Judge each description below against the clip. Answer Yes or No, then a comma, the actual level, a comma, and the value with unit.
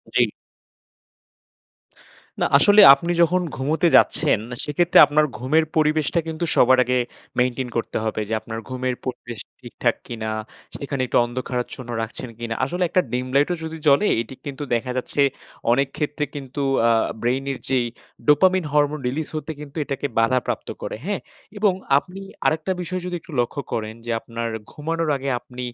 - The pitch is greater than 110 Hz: Yes, medium, 140 Hz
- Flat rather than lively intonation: No, average, 4.3 semitones